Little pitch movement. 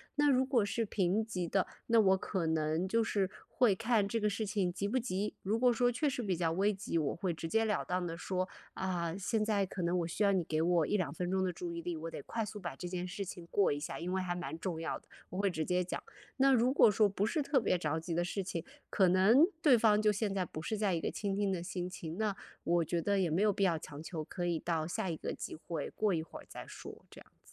No: average, 3.7 semitones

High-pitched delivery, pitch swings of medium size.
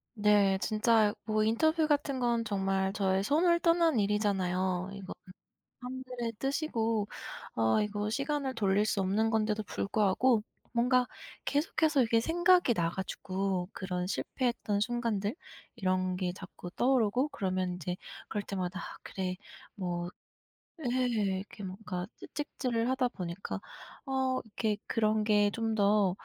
Yes: high, 215 Hz; average, 4.5 semitones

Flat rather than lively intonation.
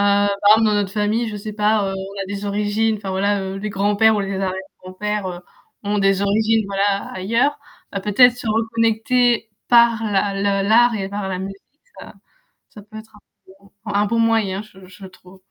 Yes: narrow, 2.0 semitones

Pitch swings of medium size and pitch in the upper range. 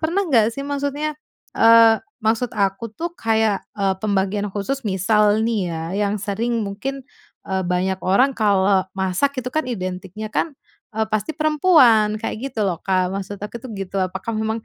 Yes: average, 4.3 semitones; high, 215 Hz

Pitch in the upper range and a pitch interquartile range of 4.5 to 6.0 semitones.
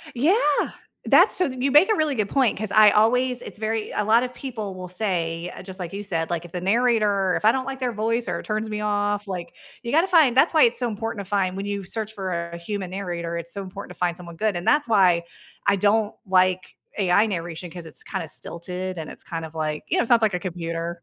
No: high, 200 Hz; average, 4.1 semitones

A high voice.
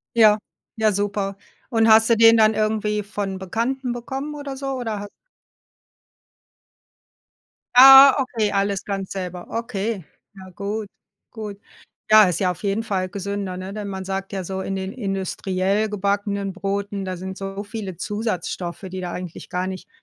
Yes: high, 200 Hz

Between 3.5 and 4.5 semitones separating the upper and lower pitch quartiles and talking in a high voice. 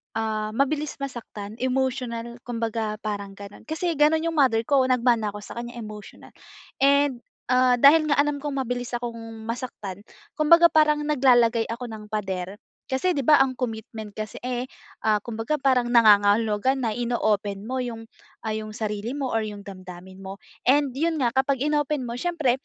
Yes: average, 4.0 semitones; high, 240 Hz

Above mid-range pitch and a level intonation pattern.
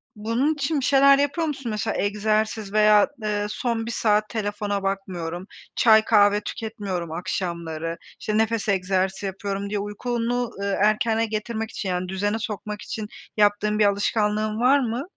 Yes: high, 210 Hz; narrow, 2.2 semitones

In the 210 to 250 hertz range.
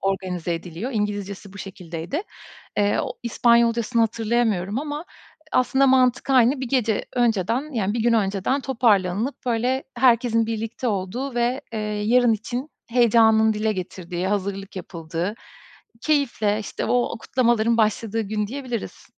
Yes: high, 225 Hz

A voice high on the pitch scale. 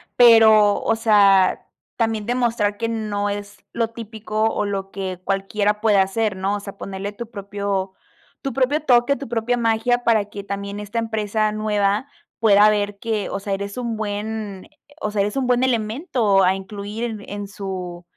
Yes: high, 210 Hz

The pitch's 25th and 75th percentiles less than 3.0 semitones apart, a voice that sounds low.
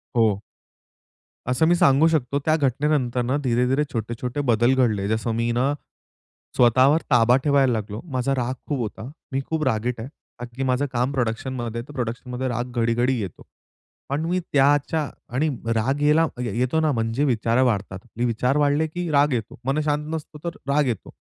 No: average, 3.6 semitones; low, 125 Hz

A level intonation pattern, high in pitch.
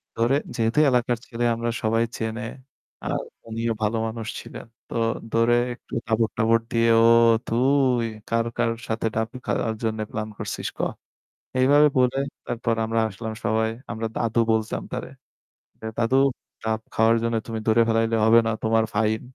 No: narrow, 1.0 semitones; low, 115 Hz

